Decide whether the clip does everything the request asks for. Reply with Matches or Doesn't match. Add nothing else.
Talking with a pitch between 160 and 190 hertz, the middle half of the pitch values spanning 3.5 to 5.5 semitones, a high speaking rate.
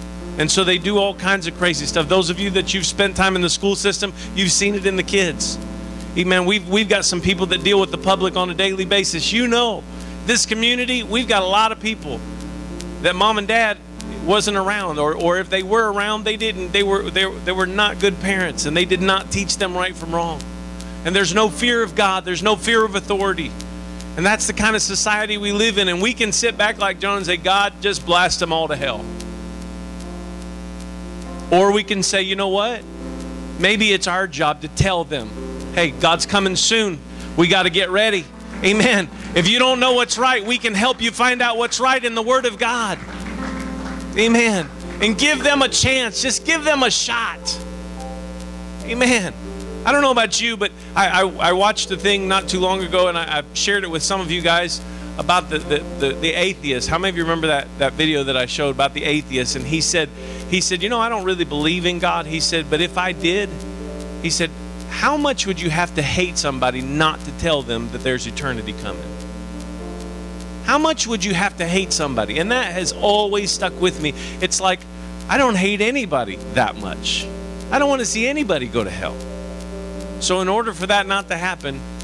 Matches